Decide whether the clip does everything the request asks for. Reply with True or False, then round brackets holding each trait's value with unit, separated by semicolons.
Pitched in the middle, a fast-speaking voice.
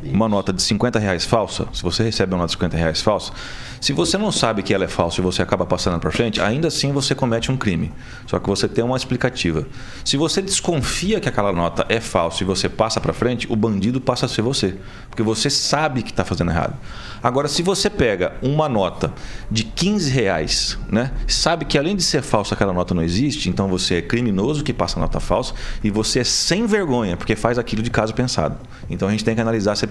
False (115 Hz; 230 wpm)